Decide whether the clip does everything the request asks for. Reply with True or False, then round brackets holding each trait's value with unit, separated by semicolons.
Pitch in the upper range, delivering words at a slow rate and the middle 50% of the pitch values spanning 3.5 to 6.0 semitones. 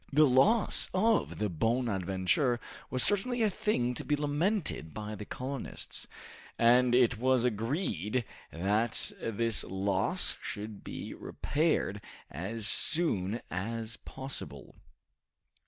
False (120 Hz; 110 wpm; 5.6 semitones)